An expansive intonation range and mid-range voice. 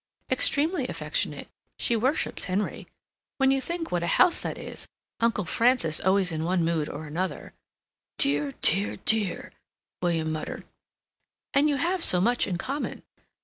No: wide, 8.3 semitones; high, 195 Hz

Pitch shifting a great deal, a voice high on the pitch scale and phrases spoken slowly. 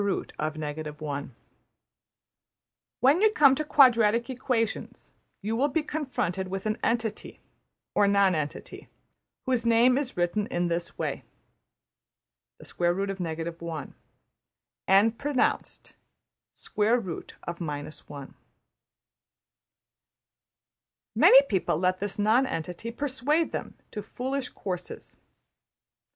Yes: wide, 6.6 semitones; high, 210 Hz; slow, 100 wpm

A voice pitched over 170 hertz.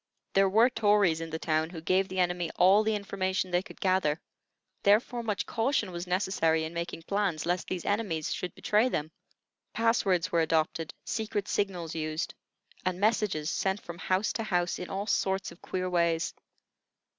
Yes: medium, 185 Hz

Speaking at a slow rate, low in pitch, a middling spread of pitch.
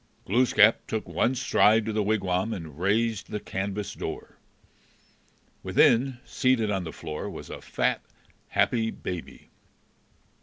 Yes: slow, 125 wpm; low, 105 Hz; average, 3.1 semitones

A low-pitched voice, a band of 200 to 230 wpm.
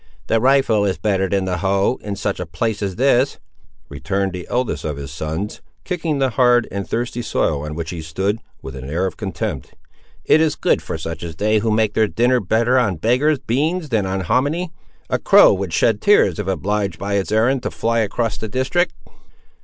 Yes: low, 105 Hz; fast, 205 wpm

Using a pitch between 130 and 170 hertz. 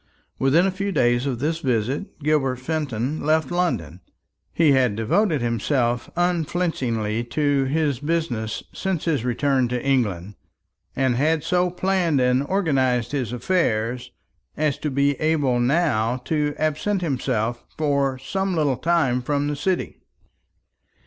Yes: medium, 140 Hz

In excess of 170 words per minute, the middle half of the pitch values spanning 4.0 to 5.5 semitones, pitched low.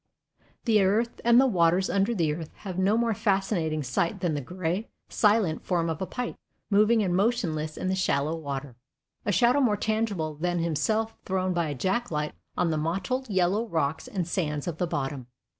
No: average, 190 wpm; average, 5.1 semitones; medium, 185 Hz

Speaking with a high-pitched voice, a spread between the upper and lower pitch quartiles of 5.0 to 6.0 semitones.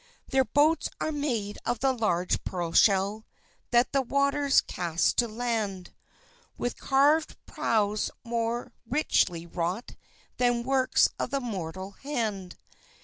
Yes: high, 235 Hz; wide, 5.6 semitones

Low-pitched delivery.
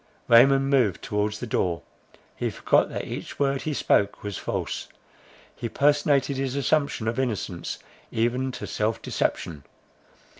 Yes: low, 125 Hz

